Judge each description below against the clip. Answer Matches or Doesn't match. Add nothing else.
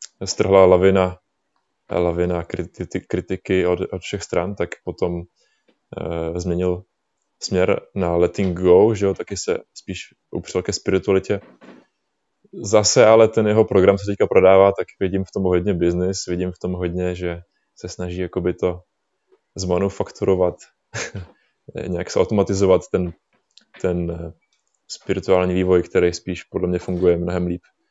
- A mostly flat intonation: Matches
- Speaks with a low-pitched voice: Matches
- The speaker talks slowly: Doesn't match